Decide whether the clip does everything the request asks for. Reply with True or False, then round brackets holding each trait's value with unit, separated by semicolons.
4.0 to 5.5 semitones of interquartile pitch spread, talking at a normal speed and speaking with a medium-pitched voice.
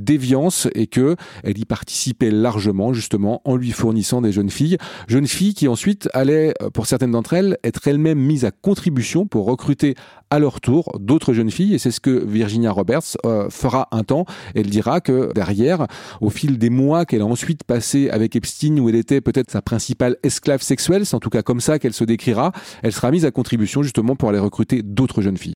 False (4.3 semitones; 210 wpm; 125 Hz)